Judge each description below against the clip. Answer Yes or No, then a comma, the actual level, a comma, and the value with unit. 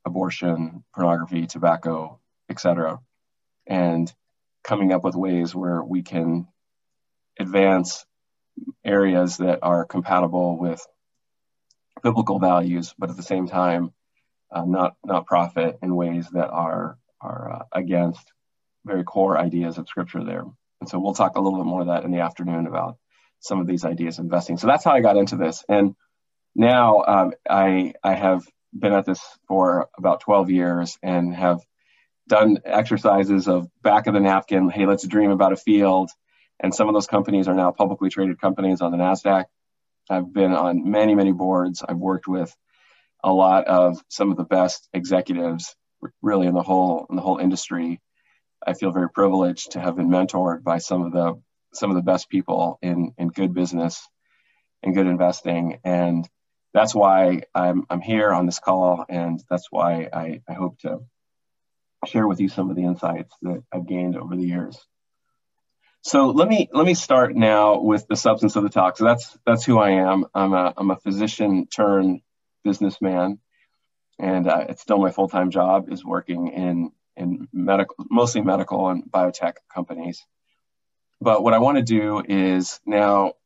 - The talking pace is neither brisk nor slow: Yes, average, 170 wpm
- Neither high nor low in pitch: No, very low, 90 Hz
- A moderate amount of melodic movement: No, narrow, 1.9 semitones